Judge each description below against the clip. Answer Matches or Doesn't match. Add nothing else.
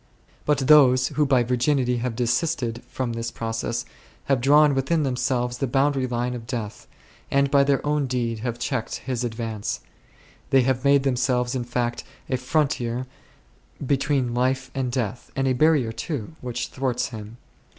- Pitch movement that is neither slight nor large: Doesn't match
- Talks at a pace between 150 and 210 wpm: Matches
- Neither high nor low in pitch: Doesn't match